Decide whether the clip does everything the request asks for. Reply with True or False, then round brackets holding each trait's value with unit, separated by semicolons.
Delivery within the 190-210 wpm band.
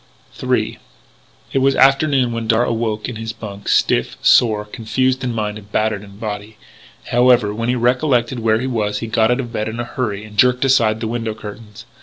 True (200 wpm)